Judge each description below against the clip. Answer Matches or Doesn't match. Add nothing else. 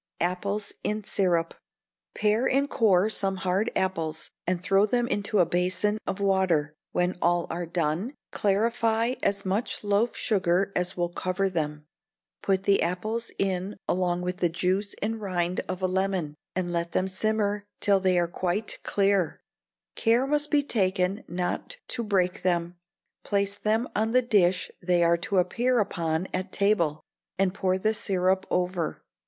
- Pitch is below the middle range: Doesn't match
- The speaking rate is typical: Matches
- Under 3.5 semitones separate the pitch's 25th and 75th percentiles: Matches